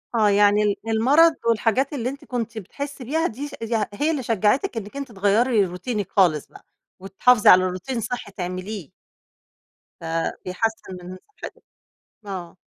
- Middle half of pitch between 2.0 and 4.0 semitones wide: No, average, 4.5 semitones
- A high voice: Yes, high, 220 Hz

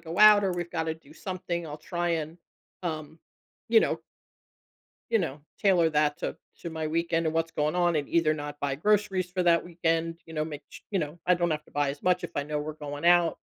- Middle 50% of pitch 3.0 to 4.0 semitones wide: No, narrow, 2.4 semitones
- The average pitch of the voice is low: No, medium, 165 Hz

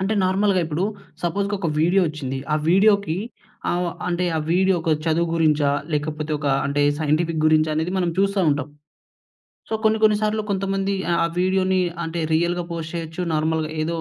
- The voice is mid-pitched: Yes, medium, 170 Hz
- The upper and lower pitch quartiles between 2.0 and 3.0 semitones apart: No, average, 3.5 semitones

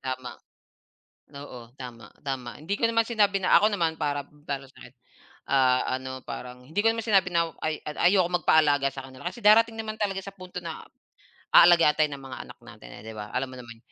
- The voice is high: No, medium, 150 Hz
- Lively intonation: Yes, wide, 6.9 semitones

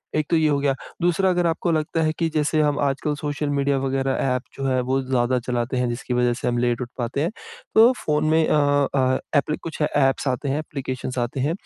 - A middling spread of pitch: Yes, average, 3.1 semitones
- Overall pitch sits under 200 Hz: Yes, medium, 140 Hz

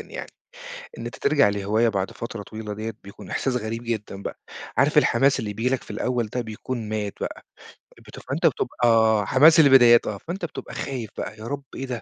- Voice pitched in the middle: No, low, 115 Hz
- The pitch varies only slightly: No, average, 3.3 semitones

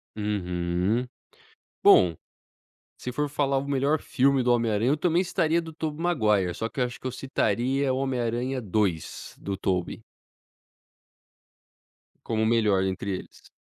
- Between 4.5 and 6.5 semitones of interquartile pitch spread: Yes, average, 5.2 semitones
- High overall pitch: No, low, 120 Hz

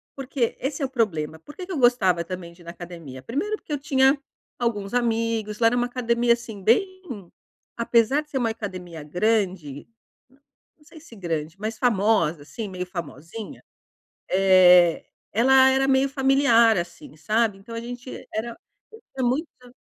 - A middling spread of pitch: No, wide, 6.3 semitones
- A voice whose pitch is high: Yes, high, 230 Hz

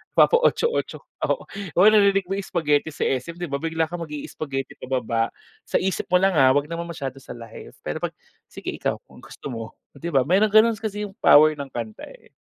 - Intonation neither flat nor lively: No, wide, 6.2 semitones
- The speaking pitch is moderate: Yes, medium, 160 Hz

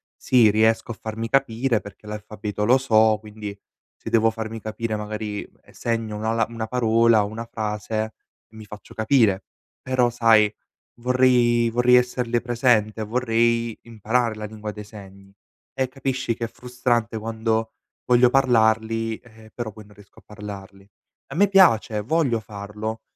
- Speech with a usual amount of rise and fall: No, narrow, 2.0 semitones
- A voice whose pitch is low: Yes, low, 110 Hz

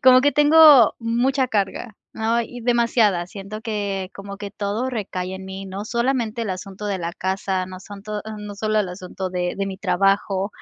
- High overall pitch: Yes, high, 205 Hz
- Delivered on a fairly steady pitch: No, average, 3.4 semitones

